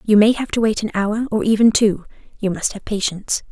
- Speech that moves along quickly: Yes, fast, 240 wpm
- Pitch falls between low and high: No, high, 210 Hz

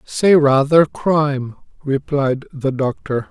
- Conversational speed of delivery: No, slow, 110 wpm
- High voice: No, medium, 140 Hz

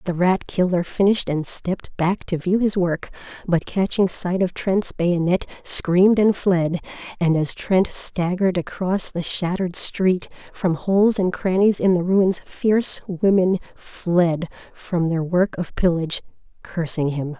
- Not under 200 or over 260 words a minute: No, average, 155 wpm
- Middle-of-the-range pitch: Yes, medium, 180 Hz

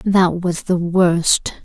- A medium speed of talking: Yes, average, 145 wpm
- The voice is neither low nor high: Yes, medium, 175 Hz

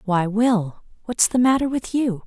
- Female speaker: Yes, female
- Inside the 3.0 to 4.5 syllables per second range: Yes, 4.2 syllables/s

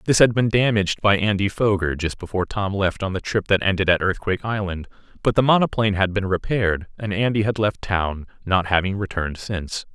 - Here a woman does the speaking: No, male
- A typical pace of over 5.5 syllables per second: Yes, 6.0 syllables/s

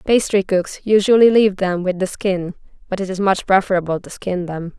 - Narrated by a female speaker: Yes, female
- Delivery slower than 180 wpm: No, average, 200 wpm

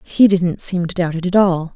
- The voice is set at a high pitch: No, medium, 180 Hz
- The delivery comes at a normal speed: No, fast, 275 wpm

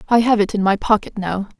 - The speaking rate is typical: No, fast, 265 wpm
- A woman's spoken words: Yes, female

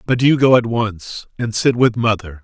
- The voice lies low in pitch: Yes, low, 115 Hz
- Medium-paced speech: No, fast, 220 wpm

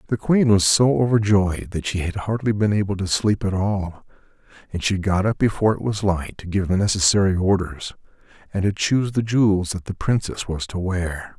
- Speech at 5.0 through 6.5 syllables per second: Yes, 5.2 syllables/s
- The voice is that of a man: Yes, male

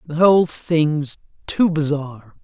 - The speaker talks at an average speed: No, slow, 125 wpm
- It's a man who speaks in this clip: No, female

